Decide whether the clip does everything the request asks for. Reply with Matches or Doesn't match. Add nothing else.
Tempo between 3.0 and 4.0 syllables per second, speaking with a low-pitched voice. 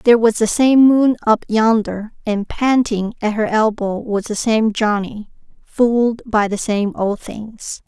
Doesn't match